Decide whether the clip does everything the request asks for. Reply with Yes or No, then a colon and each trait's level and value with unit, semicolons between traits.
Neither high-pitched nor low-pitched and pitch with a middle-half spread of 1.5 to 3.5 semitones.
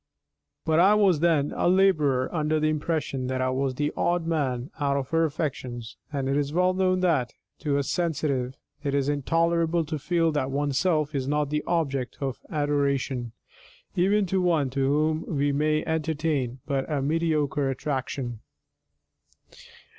Yes: medium, 150 Hz; average, 3.2 semitones